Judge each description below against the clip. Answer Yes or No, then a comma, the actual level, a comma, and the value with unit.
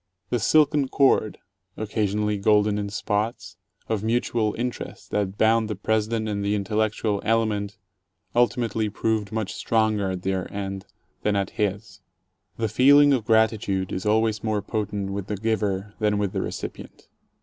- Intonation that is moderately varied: No, narrow, 1.7 semitones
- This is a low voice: Yes, low, 105 Hz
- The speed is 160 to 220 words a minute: No, average, 150 wpm